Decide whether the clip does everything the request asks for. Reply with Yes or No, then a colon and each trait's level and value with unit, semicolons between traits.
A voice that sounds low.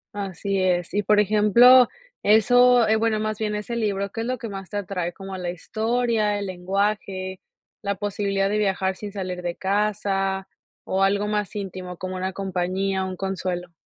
No: high, 200 Hz